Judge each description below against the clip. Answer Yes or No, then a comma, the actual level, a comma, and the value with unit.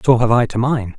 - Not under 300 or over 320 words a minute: Yes, fast, 305 wpm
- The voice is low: Yes, low, 120 Hz